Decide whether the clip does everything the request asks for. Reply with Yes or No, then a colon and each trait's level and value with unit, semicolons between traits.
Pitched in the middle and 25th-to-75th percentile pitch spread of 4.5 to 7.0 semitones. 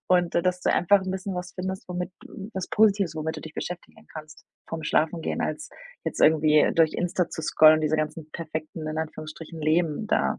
No: medium, 165 Hz; narrow, 2.5 semitones